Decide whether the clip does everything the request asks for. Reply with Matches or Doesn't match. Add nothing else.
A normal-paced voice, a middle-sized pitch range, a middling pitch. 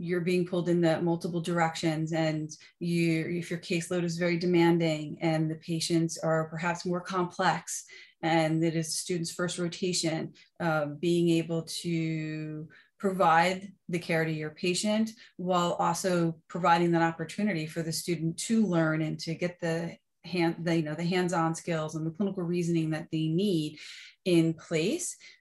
Doesn't match